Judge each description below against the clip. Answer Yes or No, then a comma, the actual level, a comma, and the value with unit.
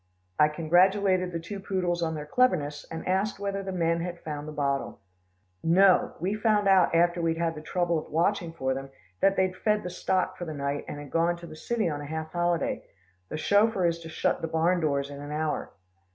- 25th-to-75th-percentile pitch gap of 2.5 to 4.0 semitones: Yes, average, 3.3 semitones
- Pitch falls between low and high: Yes, medium, 170 Hz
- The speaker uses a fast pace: Yes, fast, 220 wpm